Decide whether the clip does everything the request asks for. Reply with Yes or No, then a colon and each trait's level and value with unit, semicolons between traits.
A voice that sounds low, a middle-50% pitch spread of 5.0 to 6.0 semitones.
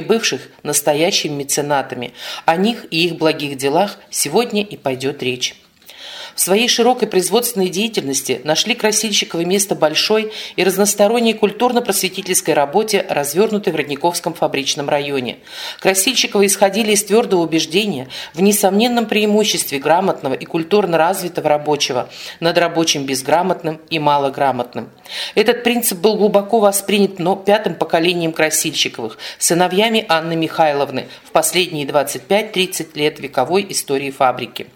No: medium, 175 Hz; average, 5.3 semitones